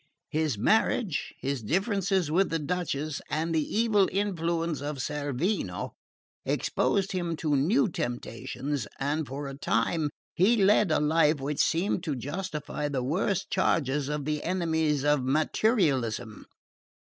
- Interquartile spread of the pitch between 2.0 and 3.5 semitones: No, average, 4.2 semitones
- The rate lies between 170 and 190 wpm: No, slow, 135 wpm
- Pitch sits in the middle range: Yes, medium, 155 Hz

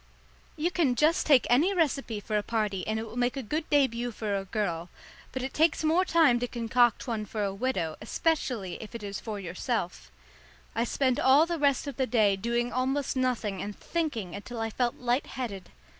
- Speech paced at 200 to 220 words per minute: Yes, fast, 205 wpm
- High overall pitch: Yes, high, 240 Hz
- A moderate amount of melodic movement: Yes, average, 4.7 semitones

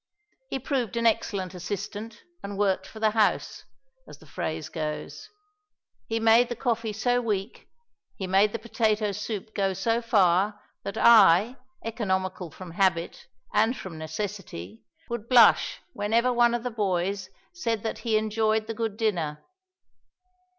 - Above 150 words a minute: No, average, 145 wpm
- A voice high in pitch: Yes, high, 210 Hz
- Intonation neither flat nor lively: Yes, average, 3.2 semitones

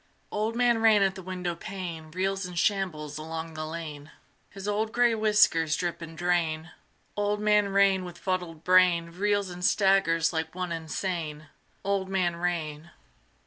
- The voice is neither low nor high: Yes, medium, 180 Hz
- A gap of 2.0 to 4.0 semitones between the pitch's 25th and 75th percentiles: Yes, average, 3.3 semitones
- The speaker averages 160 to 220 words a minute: No, average, 150 wpm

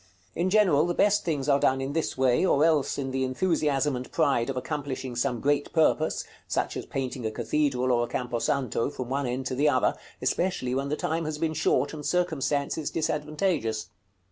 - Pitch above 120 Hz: Yes, medium, 140 Hz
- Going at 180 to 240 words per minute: Yes, average, 195 wpm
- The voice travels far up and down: No, average, 3.4 semitones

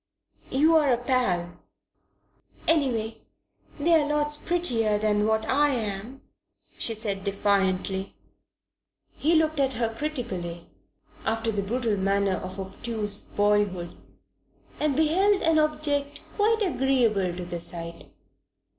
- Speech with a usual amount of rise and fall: No, wide, 6.9 semitones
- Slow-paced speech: Yes, slow, 110 wpm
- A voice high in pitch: Yes, high, 225 Hz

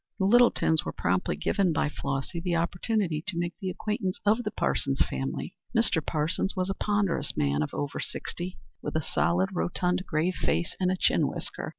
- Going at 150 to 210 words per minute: Yes, average, 185 wpm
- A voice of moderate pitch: Yes, medium, 175 Hz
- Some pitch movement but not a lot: Yes, average, 3.9 semitones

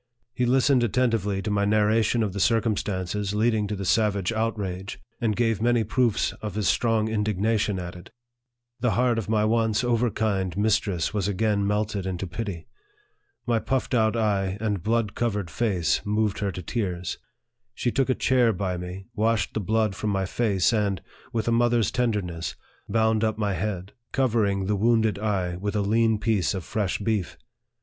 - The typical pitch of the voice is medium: No, low, 105 Hz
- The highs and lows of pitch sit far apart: No, average, 2.7 semitones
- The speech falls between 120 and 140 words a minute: No, average, 175 wpm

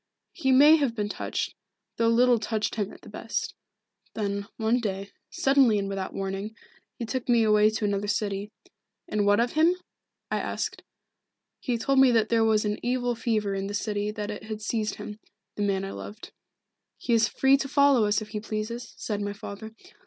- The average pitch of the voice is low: No, high, 215 Hz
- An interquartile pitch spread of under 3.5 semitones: Yes, narrow, 2.6 semitones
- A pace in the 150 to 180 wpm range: No, average, 195 wpm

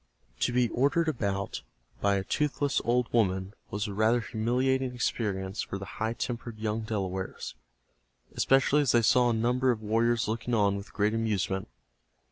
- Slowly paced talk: No, average, 160 wpm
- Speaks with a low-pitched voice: Yes, low, 115 Hz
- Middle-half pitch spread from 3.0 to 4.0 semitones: Yes, average, 3.3 semitones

